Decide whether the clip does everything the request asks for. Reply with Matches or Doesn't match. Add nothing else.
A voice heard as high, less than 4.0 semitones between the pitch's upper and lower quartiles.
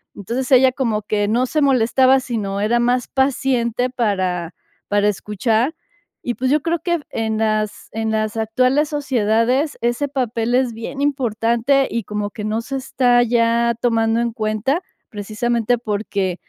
Matches